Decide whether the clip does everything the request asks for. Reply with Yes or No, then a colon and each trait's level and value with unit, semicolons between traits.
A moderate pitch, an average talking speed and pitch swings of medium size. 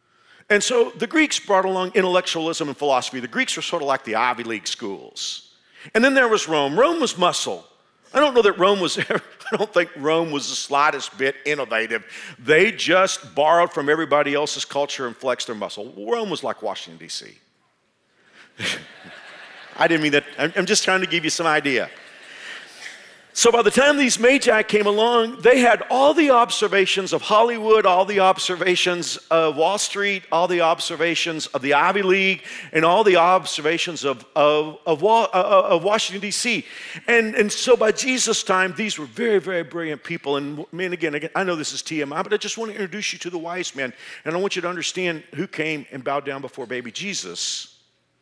No: medium, 175 Hz; average, 190 wpm; wide, 5.7 semitones